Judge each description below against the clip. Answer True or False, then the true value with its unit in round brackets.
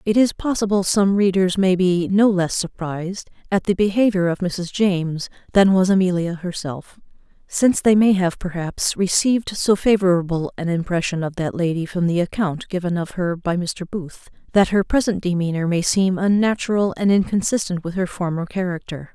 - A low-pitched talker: False (185 Hz)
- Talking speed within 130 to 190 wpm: True (170 wpm)